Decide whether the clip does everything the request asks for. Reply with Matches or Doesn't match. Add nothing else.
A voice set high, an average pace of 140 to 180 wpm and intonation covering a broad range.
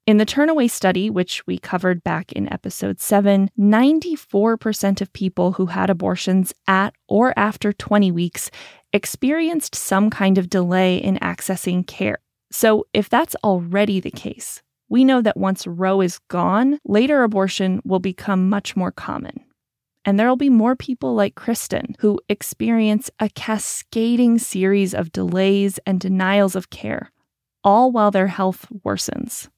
Doesn't match